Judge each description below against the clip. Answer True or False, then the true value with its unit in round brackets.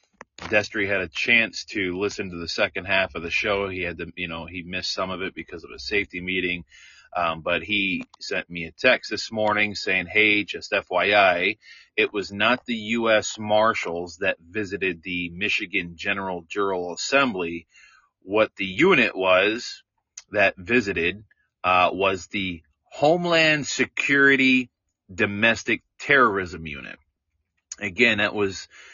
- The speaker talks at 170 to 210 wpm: False (145 wpm)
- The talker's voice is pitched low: True (95 Hz)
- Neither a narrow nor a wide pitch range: True (3.6 semitones)